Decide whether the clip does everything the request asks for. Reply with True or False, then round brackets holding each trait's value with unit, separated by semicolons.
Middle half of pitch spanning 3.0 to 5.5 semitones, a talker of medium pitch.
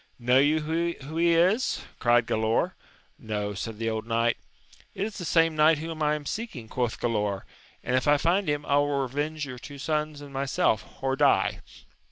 True (4.8 semitones; 145 Hz)